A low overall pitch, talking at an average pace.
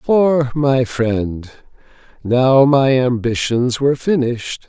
No: low, 130 Hz; slow, 105 wpm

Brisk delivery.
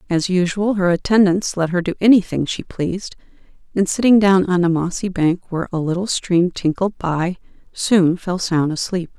No: average, 175 wpm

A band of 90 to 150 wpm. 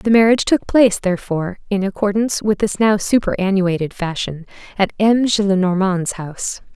Yes: average, 140 wpm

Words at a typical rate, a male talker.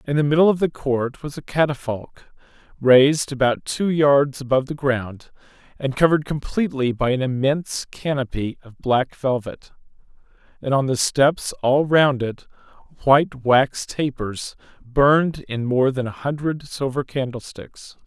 Yes: average, 145 wpm; male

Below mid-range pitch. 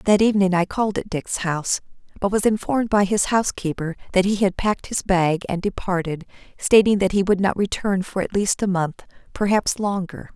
No: high, 195 Hz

